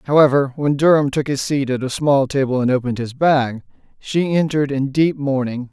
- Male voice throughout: Yes, male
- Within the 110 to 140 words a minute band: No, average, 200 wpm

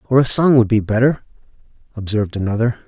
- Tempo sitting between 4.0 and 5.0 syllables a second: No, 6.5 syllables/s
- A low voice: Yes, low, 115 Hz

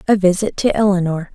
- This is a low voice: No, high, 190 Hz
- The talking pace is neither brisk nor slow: Yes, average, 180 wpm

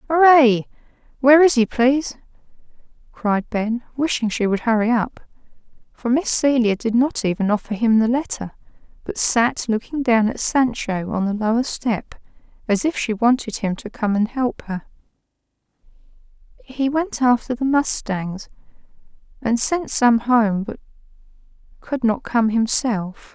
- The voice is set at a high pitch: Yes, high, 235 Hz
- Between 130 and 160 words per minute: Yes, average, 145 wpm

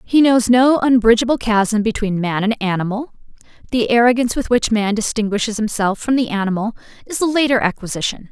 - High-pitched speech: Yes, high, 225 Hz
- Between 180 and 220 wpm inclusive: No, average, 165 wpm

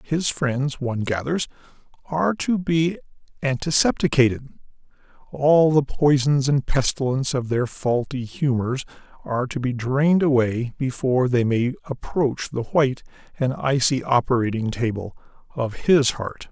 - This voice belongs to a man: Yes, male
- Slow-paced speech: Yes, slow, 125 wpm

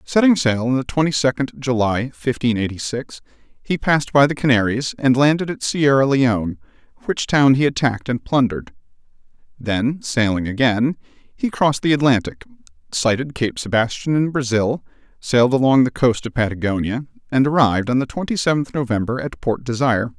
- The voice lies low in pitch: Yes, low, 125 Hz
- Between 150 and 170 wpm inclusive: Yes, average, 165 wpm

